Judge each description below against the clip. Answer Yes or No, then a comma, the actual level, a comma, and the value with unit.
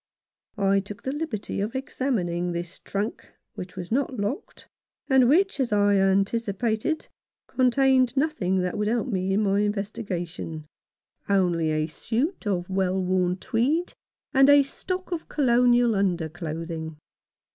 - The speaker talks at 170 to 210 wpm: No, slow, 135 wpm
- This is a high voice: Yes, high, 205 Hz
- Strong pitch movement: Yes, wide, 6.0 semitones